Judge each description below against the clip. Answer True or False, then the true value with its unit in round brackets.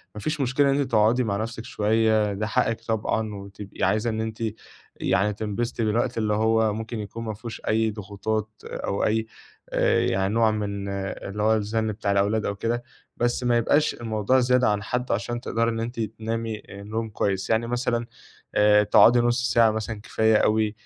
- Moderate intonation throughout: False (1.7 semitones)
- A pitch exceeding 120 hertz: False (110 Hz)